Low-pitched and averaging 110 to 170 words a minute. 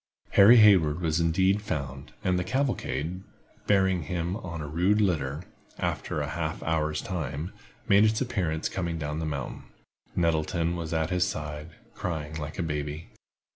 Yes: very low, 85 Hz; average, 155 wpm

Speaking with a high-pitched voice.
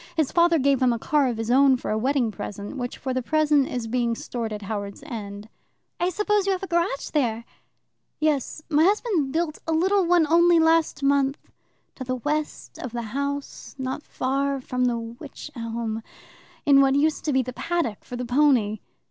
Yes: very high, 275 Hz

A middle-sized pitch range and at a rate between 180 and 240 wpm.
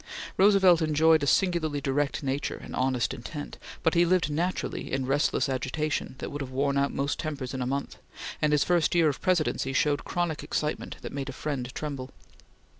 Yes: average, 3.0 semitones; average, 190 wpm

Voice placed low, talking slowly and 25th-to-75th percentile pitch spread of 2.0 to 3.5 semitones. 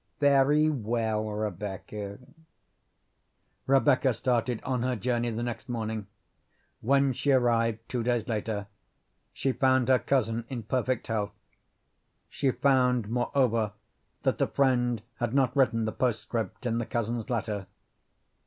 Yes: low, 120 Hz; slow, 125 wpm; average, 2.7 semitones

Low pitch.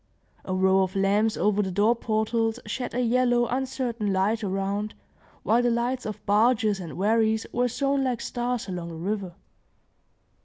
No: high, 220 Hz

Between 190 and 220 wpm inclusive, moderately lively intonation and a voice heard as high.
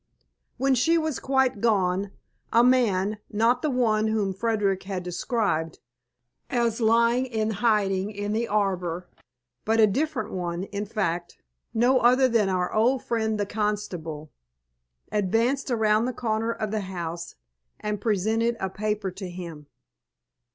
No: average, 140 wpm; average, 3.5 semitones; high, 215 Hz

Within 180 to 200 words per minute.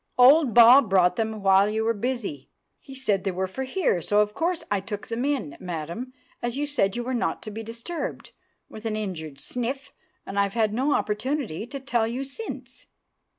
Yes: average, 195 wpm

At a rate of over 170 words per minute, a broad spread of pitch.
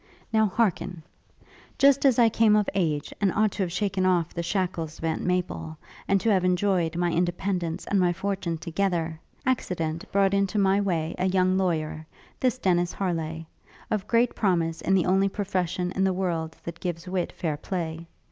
No: average, 180 wpm; average, 2.8 semitones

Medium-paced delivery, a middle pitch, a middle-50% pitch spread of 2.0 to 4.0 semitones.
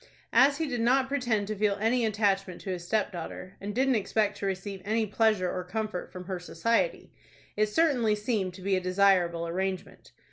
No: average, 185 wpm; high, 205 Hz; average, 3.5 semitones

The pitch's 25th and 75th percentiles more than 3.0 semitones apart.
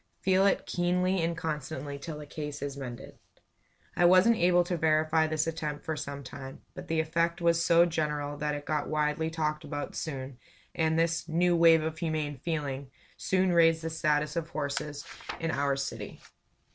No: narrow, 2.4 semitones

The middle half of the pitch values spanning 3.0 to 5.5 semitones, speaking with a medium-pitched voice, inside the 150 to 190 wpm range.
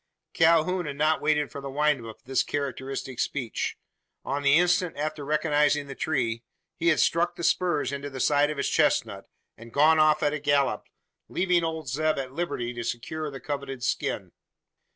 No: narrow, 2.6 semitones; medium, 145 Hz; average, 185 wpm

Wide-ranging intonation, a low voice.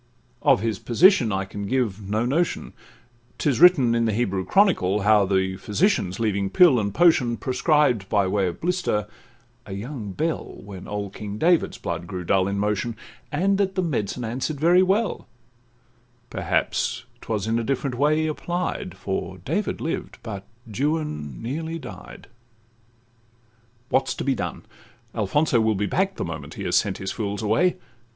Yes: wide, 7.4 semitones; low, 115 Hz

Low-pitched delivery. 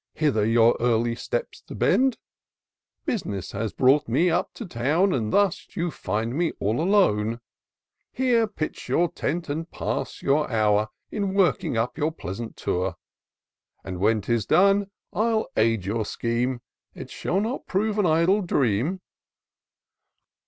No: medium, 145 Hz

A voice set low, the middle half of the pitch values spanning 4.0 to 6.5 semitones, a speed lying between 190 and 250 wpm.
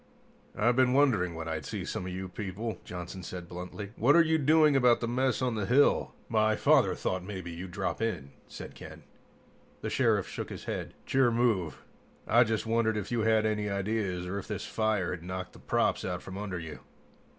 Yes: low, 105 Hz; average, 4.5 semitones; fast, 205 wpm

